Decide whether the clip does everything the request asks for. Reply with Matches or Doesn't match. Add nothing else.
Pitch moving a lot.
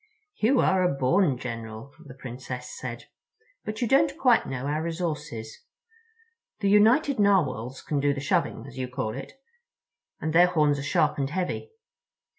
Matches